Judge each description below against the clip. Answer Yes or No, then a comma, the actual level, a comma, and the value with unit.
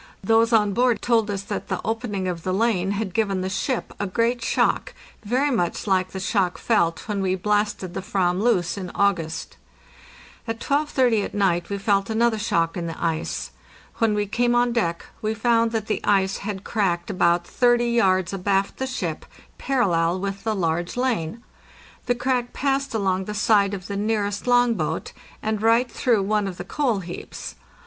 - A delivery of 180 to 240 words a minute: Yes, average, 185 wpm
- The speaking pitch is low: No, high, 205 Hz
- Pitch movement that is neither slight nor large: Yes, average, 3.8 semitones